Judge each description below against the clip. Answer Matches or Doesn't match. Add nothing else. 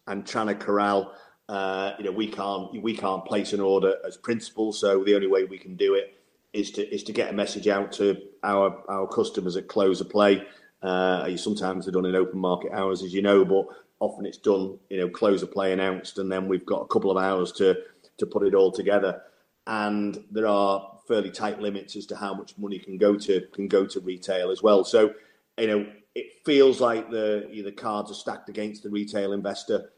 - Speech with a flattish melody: Matches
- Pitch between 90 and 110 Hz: Matches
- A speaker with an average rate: Doesn't match